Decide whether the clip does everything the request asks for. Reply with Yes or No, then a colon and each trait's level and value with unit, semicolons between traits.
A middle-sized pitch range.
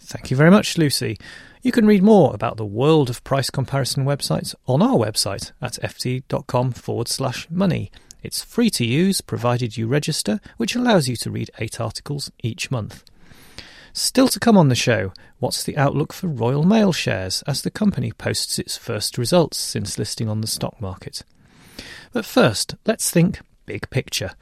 No: wide, 7.1 semitones